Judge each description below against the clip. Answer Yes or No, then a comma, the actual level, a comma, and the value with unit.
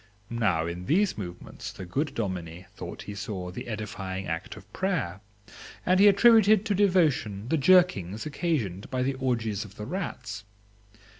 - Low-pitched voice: Yes, low, 110 Hz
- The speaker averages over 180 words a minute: No, average, 155 wpm